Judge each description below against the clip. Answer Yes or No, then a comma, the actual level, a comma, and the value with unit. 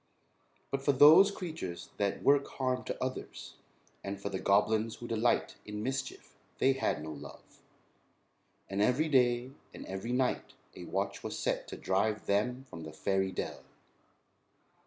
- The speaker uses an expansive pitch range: No, average, 5.0 semitones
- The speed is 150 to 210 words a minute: Yes, average, 155 wpm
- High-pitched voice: No, low, 120 Hz